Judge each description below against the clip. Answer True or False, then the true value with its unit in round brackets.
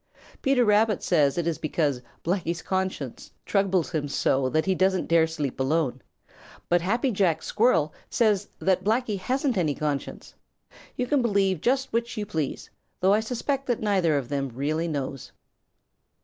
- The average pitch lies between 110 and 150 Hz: False (185 Hz)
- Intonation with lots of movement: True (5.9 semitones)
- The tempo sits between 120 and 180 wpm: True (165 wpm)